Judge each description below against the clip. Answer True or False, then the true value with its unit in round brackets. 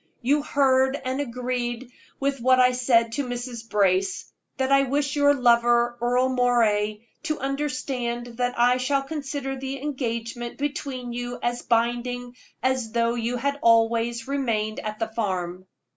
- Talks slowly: False (145 wpm)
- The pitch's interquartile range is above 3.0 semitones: False (2.5 semitones)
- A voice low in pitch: False (245 Hz)